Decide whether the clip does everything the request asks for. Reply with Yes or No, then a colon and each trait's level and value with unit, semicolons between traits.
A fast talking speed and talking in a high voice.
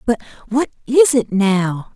No: slow, 125 wpm; high, 230 Hz